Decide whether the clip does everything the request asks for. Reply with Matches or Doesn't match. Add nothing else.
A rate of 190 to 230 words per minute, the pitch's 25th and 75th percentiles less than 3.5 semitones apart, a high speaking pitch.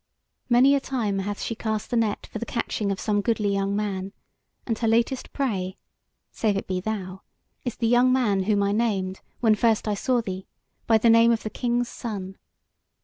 Matches